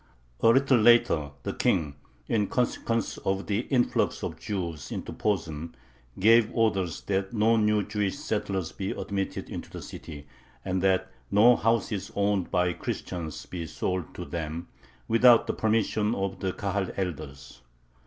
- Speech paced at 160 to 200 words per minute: No, average, 145 wpm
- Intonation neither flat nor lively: Yes, average, 3.8 semitones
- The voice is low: Yes, low, 100 Hz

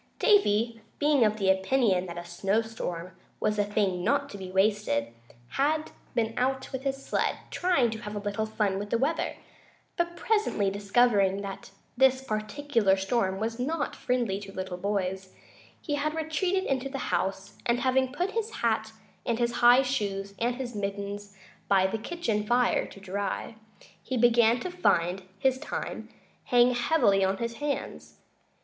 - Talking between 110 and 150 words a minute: No, average, 165 wpm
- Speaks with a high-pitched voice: Yes, high, 225 Hz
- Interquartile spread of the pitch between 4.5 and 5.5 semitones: Yes, average, 5.1 semitones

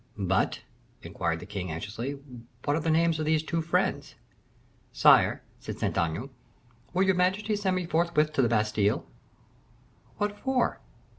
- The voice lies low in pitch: No, medium, 155 Hz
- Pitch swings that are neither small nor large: No, wide, 9.0 semitones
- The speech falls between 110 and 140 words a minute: No, average, 150 wpm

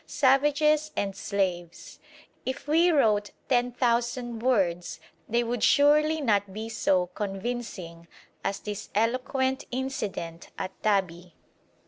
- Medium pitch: No, high, 230 Hz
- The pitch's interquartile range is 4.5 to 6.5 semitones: Yes, average, 5.3 semitones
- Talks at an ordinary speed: No, slow, 110 wpm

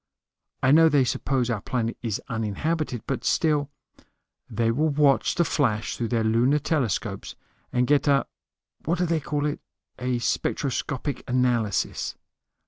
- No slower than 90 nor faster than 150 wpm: Yes, average, 145 wpm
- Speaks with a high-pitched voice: No, low, 130 Hz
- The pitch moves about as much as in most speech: Yes, average, 4.2 semitones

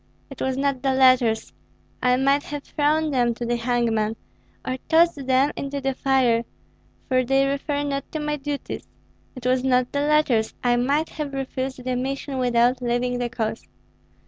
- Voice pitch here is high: Yes, very high, 260 Hz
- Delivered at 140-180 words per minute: Yes, average, 170 wpm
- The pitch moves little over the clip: Yes, narrow, 2.3 semitones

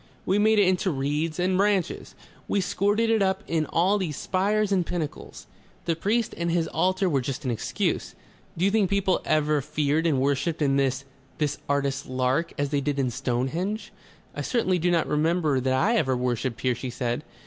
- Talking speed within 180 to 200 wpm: Yes, average, 195 wpm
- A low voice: No, medium, 160 Hz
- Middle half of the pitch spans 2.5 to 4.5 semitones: No, wide, 5.6 semitones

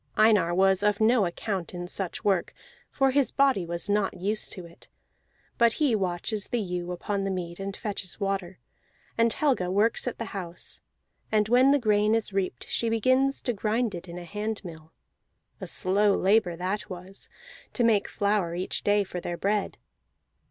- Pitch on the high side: Yes, high, 200 Hz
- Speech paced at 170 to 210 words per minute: Yes, average, 175 wpm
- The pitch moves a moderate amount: Yes, average, 3.5 semitones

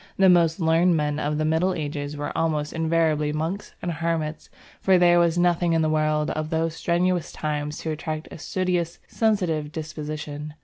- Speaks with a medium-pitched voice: Yes, medium, 160 Hz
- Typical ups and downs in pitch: No, narrow, 2.2 semitones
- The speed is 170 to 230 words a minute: Yes, average, 175 wpm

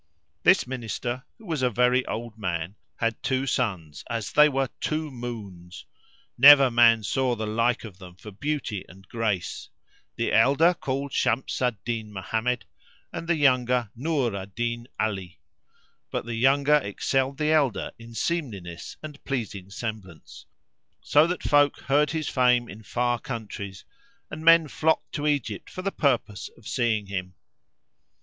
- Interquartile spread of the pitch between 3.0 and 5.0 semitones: Yes, average, 4.7 semitones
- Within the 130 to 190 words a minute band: Yes, average, 155 wpm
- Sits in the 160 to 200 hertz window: No, low, 120 Hz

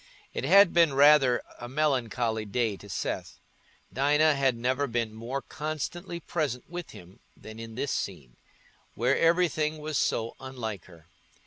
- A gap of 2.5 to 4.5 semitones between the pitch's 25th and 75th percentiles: No, average, 5.2 semitones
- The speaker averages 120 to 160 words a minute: Yes, average, 145 wpm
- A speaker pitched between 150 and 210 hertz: No, low, 130 Hz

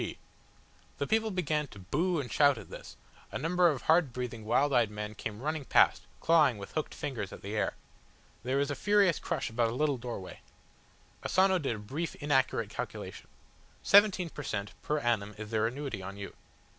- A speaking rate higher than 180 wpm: Yes, average, 190 wpm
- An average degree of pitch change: No, wide, 6.4 semitones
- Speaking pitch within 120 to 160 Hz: Yes, low, 135 Hz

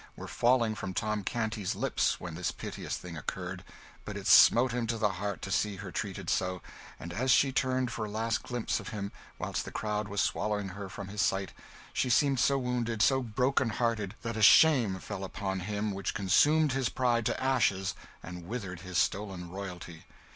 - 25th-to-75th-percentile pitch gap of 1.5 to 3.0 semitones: No, average, 4.0 semitones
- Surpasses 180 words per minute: Yes, average, 195 wpm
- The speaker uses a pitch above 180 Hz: No, low, 105 Hz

